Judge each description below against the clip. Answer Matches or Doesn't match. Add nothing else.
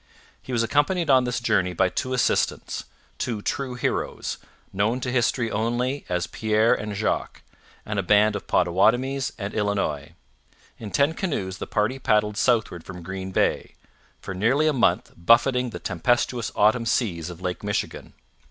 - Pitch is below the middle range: Matches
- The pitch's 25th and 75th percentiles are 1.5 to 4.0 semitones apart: Doesn't match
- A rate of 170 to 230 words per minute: Doesn't match